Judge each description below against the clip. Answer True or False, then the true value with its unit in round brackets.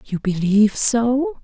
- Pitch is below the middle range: False (230 Hz)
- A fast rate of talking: False (125 wpm)